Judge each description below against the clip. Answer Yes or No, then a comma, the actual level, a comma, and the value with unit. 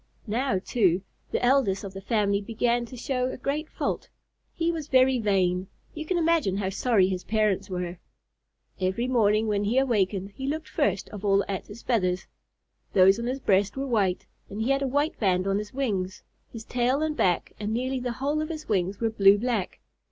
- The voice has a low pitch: No, high, 220 Hz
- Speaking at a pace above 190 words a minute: Yes, average, 200 wpm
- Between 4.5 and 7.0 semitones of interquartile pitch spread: Yes, average, 4.9 semitones